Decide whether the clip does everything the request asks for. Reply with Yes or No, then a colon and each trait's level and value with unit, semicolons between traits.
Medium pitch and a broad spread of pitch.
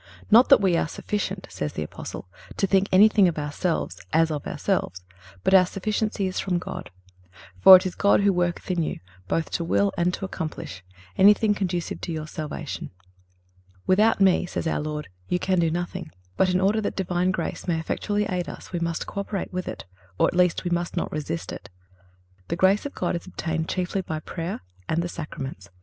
No: medium, 180 Hz; average, 3.0 semitones